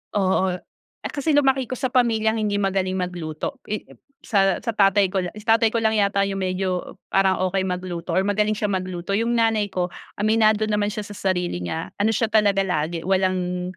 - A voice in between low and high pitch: No, high, 200 Hz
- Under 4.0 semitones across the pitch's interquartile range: Yes, average, 2.8 semitones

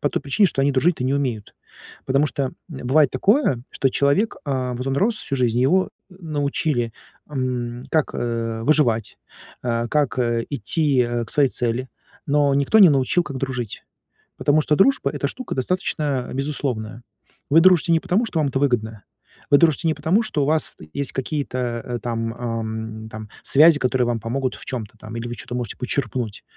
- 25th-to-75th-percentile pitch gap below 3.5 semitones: No, average, 3.9 semitones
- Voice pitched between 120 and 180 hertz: Yes, low, 135 Hz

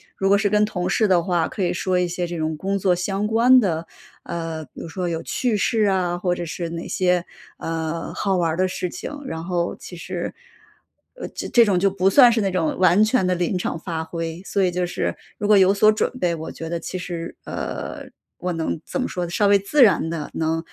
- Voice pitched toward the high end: No, medium, 180 Hz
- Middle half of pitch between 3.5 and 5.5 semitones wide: No, average, 2.9 semitones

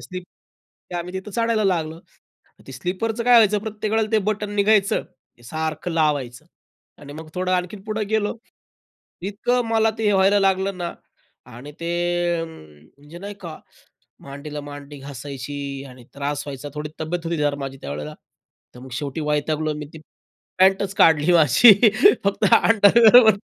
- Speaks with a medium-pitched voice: Yes, medium, 170 Hz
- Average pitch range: No, wide, 5.9 semitones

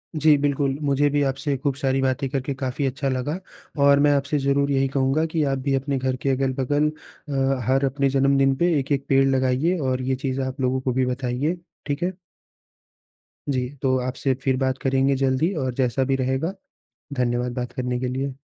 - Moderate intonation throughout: No, narrow, 1.4 semitones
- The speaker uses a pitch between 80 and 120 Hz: No, low, 135 Hz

